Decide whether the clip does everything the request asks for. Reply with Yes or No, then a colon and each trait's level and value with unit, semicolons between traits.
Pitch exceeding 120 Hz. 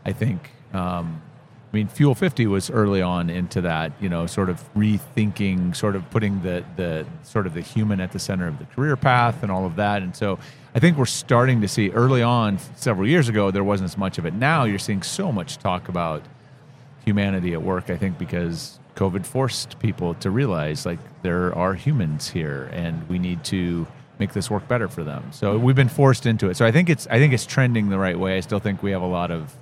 No: low, 100 Hz